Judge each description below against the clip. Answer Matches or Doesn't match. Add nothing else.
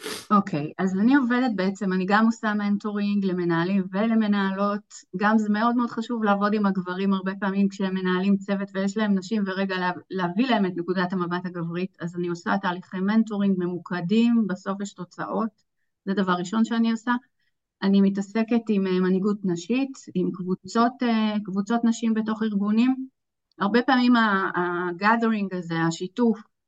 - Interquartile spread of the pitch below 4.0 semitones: Matches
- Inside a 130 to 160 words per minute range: Matches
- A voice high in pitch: Matches